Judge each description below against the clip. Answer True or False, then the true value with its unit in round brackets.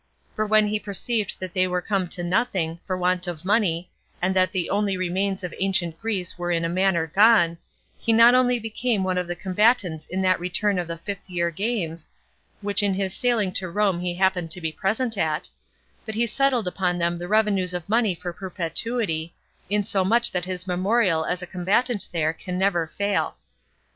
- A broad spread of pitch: False (3.0 semitones)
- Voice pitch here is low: False (185 Hz)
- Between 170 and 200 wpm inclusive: True (190 wpm)